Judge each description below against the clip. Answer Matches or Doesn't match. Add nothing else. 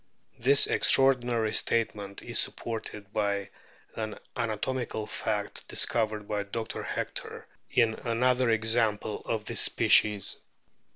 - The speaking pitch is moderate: Doesn't match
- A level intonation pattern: Matches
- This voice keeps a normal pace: Doesn't match